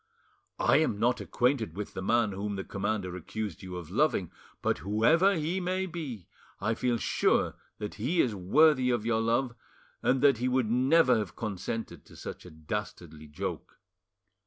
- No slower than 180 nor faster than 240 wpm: No, average, 170 wpm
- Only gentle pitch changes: No, average, 4.8 semitones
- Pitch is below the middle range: Yes, low, 115 Hz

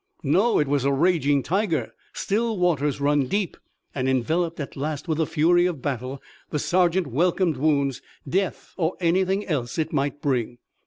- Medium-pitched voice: Yes, medium, 155 Hz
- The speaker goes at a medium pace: Yes, average, 165 wpm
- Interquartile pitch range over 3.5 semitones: Yes, average, 4.2 semitones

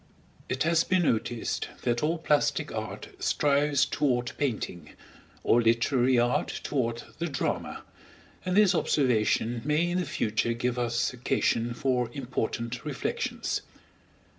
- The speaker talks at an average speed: No, slow, 125 wpm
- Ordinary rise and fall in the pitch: Yes, average, 4.0 semitones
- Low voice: Yes, low, 125 Hz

